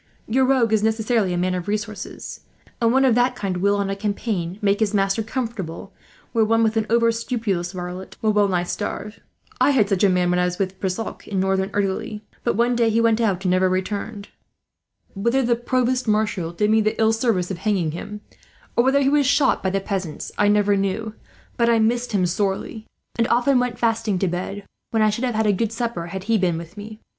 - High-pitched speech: Yes, high, 210 Hz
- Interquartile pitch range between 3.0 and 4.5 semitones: Yes, average, 3.3 semitones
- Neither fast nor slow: No, fast, 225 wpm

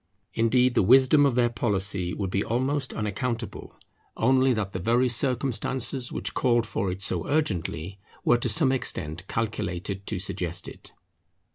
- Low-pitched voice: Yes, low, 115 Hz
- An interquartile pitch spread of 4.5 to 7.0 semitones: Yes, average, 4.8 semitones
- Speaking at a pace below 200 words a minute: Yes, average, 150 wpm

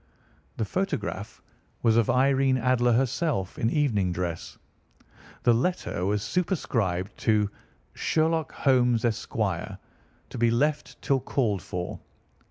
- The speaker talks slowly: Yes, slow, 115 wpm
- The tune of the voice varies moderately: Yes, average, 4.8 semitones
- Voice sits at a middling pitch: No, low, 120 Hz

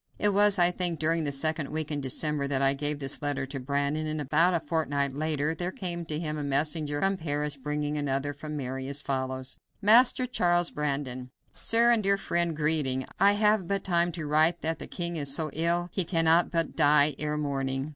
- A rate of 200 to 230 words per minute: Yes, fast, 205 wpm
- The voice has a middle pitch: Yes, medium, 150 Hz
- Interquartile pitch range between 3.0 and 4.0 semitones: Yes, average, 3.3 semitones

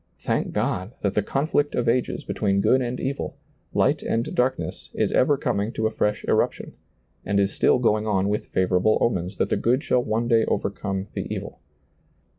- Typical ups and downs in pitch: Yes, average, 3.9 semitones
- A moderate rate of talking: Yes, average, 185 wpm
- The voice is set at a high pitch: No, low, 110 Hz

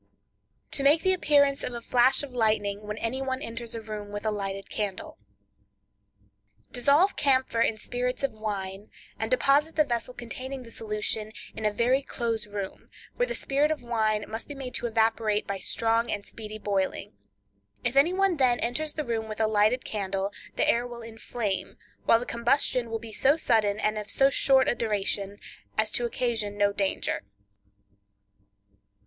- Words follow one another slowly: No, average, 175 wpm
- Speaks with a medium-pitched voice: No, high, 225 Hz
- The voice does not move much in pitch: No, average, 3.7 semitones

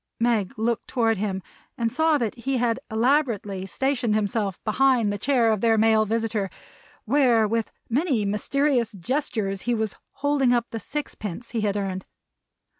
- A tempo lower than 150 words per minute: No, average, 160 wpm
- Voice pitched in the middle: No, high, 225 Hz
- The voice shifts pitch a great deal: No, average, 3.4 semitones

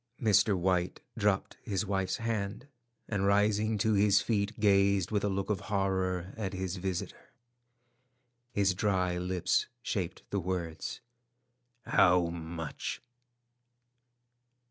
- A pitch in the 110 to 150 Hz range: No, very low, 95 Hz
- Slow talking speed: Yes, slow, 115 wpm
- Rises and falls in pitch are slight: Yes, narrow, 1.9 semitones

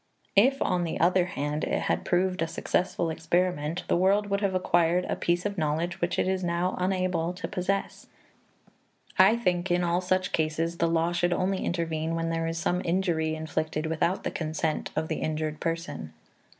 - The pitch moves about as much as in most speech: No, narrow, 2.2 semitones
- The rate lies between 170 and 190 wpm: Yes, average, 185 wpm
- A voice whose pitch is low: No, medium, 175 Hz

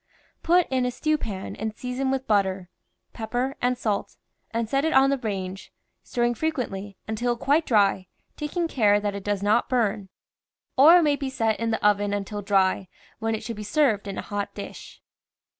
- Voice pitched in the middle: No, high, 225 Hz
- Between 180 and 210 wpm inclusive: Yes, average, 195 wpm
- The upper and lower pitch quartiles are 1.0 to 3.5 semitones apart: No, average, 4.6 semitones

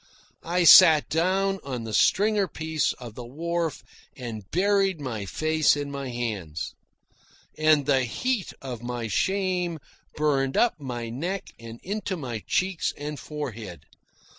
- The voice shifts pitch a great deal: Yes, wide, 6.8 semitones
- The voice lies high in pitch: No, medium, 145 Hz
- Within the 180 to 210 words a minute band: No, average, 140 wpm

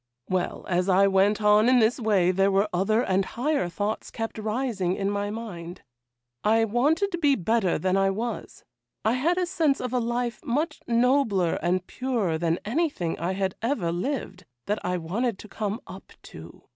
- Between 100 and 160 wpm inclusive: No, average, 185 wpm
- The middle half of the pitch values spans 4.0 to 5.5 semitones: Yes, average, 4.7 semitones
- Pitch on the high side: Yes, high, 210 Hz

